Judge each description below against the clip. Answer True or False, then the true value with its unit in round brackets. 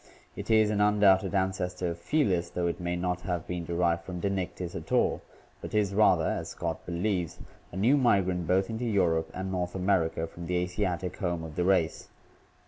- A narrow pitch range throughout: True (2.3 semitones)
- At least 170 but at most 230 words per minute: True (190 wpm)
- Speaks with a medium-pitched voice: False (90 Hz)